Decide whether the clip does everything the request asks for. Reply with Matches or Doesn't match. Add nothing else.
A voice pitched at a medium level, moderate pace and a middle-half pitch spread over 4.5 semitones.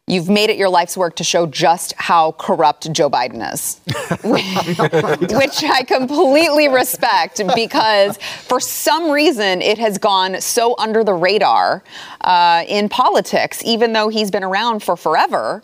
Doesn't match